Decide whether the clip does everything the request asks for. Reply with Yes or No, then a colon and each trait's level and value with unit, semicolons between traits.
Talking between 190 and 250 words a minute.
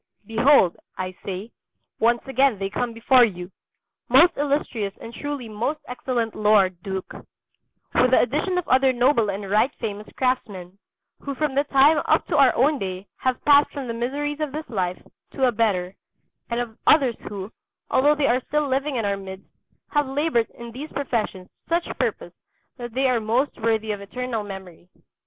No: average, 180 wpm